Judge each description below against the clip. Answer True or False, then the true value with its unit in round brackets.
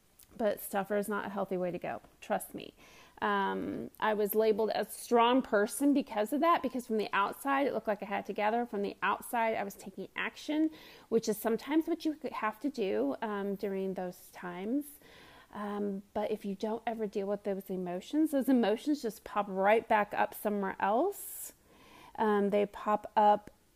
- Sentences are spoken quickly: False (185 wpm)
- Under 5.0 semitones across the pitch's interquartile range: True (3.7 semitones)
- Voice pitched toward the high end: True (215 Hz)